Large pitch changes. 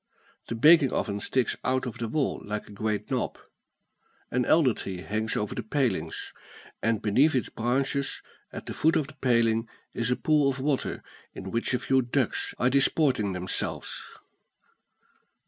No: average, 3.8 semitones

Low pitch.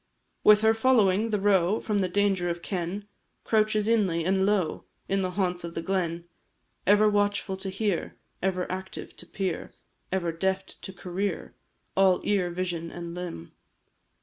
No: high, 190 Hz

